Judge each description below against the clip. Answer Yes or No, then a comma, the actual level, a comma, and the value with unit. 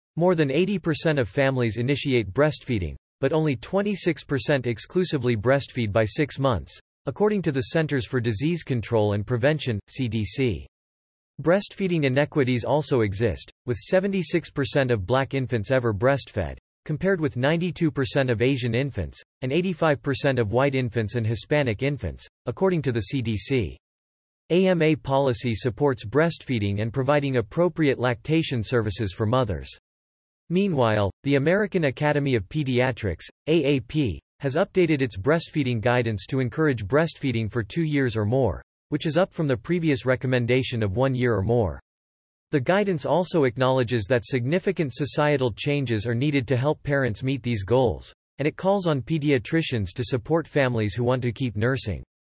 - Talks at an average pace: Yes, average, 145 wpm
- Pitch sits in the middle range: No, low, 130 Hz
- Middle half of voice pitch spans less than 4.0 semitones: No, average, 4.6 semitones